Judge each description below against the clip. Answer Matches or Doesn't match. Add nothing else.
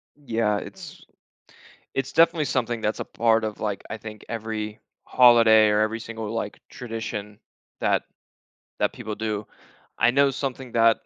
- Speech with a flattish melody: Matches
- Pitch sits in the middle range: Doesn't match